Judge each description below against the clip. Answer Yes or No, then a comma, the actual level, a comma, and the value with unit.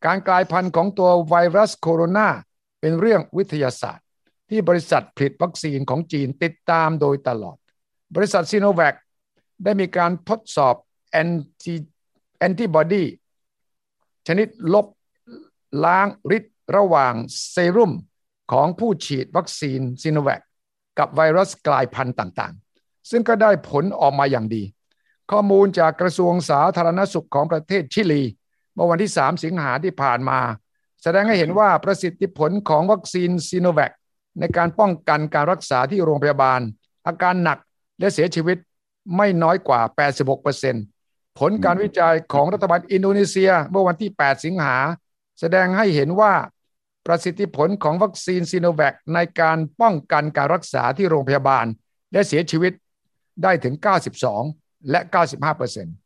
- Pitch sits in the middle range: Yes, medium, 170 Hz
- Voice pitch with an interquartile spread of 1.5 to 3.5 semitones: No, average, 4.8 semitones